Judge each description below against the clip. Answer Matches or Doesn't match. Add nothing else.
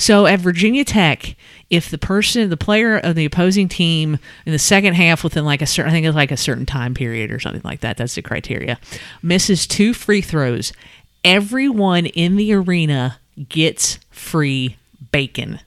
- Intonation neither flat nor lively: Doesn't match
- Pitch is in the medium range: Matches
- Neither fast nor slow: Matches